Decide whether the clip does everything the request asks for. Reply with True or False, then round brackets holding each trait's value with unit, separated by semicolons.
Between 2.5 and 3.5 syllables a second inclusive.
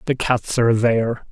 False (5.3 syllables/s)